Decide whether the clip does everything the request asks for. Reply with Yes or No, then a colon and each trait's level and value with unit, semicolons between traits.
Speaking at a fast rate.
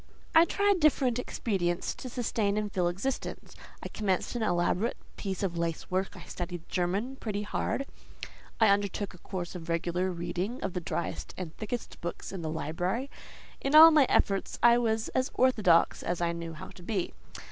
No: average, 180 wpm